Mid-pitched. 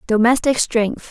No: high, 230 Hz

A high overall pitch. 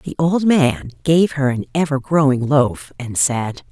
No: medium, 140 Hz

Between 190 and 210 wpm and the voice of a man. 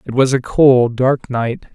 Yes: fast, 205 wpm; male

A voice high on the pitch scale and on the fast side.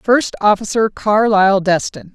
No: high, 205 Hz; slow, 110 wpm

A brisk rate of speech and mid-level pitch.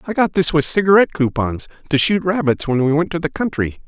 Yes: fast, 230 wpm; medium, 160 Hz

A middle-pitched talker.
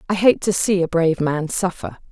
Yes: medium, 180 Hz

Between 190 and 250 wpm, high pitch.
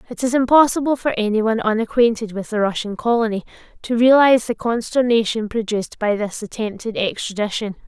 No: average, 145 wpm; high, 225 Hz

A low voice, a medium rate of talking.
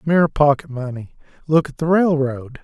No: medium, 145 Hz; average, 160 wpm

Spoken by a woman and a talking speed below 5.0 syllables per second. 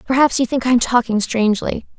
No: female; 6.4 syllables/s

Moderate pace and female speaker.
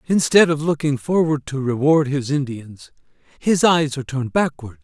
No: average, 160 wpm; male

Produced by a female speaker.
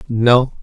No: male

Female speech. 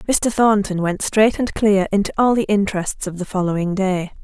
Yes: female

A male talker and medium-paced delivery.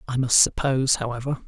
Yes: male; average, 160 wpm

